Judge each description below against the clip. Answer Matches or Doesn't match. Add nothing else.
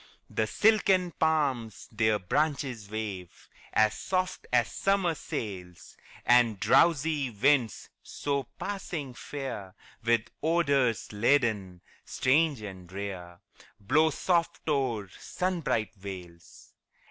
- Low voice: Matches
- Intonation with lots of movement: Matches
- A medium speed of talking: Doesn't match